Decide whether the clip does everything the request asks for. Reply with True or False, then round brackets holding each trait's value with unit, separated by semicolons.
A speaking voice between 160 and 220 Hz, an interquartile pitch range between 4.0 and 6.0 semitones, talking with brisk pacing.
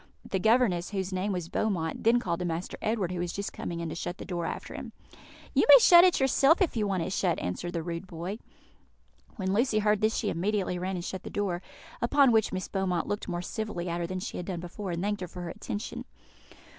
False (190 Hz; 3.5 semitones; 240 wpm)